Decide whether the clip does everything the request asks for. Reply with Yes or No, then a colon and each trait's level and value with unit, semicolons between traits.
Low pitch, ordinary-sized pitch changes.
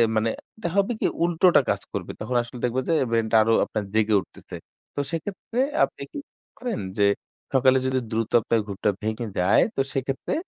No: low, 125 Hz; wide, 6.8 semitones